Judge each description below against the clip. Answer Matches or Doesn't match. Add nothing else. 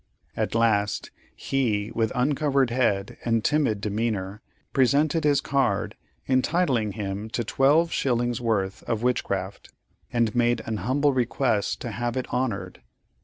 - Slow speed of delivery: Matches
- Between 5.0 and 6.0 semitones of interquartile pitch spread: Doesn't match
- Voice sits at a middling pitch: Doesn't match